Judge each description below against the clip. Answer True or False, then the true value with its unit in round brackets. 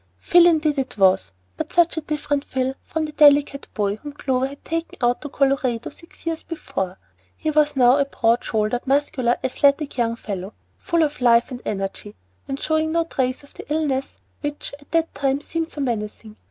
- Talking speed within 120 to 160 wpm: False (190 wpm)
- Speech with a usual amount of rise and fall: True (4.1 semitones)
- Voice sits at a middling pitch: False (275 Hz)